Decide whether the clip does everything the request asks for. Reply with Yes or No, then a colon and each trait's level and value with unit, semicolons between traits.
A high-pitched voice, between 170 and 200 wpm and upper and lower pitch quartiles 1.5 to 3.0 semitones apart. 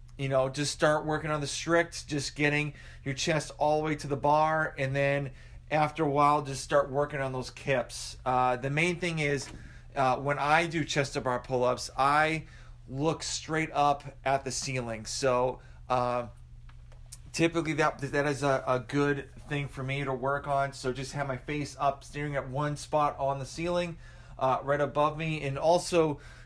No: medium, 140 Hz; average, 190 wpm; narrow, 2.4 semitones